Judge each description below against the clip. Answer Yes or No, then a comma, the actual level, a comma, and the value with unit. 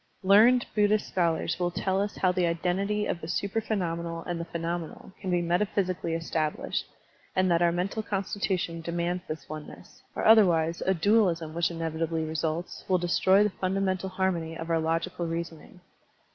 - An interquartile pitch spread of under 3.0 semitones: Yes, narrow, 2.4 semitones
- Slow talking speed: No, average, 175 wpm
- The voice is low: No, medium, 175 Hz